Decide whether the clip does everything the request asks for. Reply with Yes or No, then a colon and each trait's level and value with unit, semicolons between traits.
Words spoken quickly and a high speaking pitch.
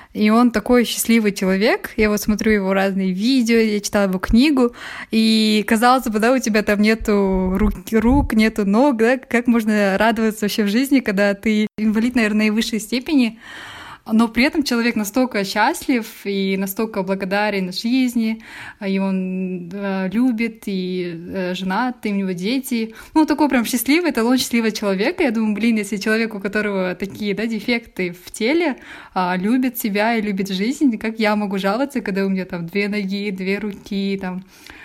Yes: fast, 165 wpm; high, 215 Hz